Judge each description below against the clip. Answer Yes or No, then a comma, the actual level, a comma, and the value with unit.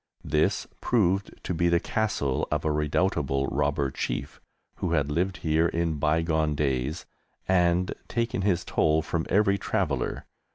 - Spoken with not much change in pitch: No, average, 3.6 semitones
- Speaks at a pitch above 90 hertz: No, very low, 80 Hz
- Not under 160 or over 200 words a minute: No, average, 140 wpm